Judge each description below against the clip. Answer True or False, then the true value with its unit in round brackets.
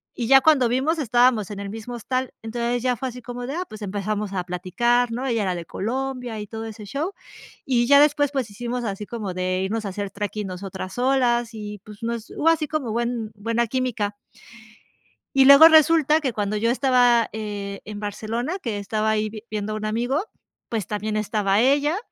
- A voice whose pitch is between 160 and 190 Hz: False (230 Hz)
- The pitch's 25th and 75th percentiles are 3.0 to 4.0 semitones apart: True (3.6 semitones)